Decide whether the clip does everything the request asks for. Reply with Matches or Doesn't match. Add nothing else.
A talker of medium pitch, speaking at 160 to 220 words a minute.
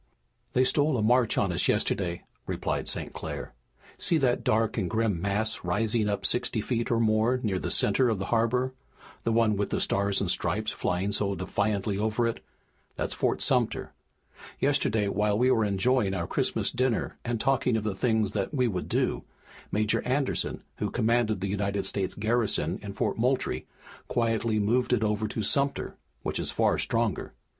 Doesn't match